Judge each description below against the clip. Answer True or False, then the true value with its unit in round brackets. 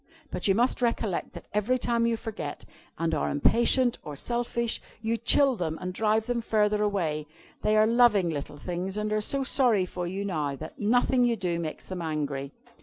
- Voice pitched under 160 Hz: False (210 Hz)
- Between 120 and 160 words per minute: False (190 wpm)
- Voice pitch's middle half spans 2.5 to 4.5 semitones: False (5.6 semitones)